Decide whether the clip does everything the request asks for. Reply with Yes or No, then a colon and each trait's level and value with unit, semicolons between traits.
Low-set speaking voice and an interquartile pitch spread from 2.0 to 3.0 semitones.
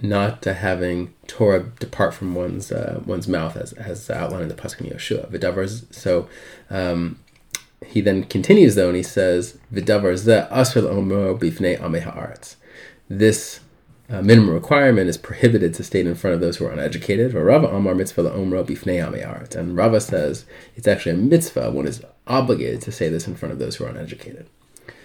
No: low, 100 Hz; average, 3.4 semitones